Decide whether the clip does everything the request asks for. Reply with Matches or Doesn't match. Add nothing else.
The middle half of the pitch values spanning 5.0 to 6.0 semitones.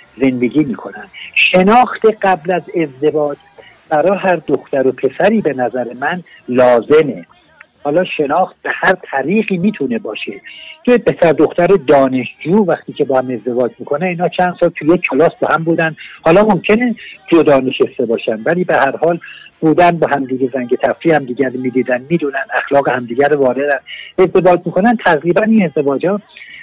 Matches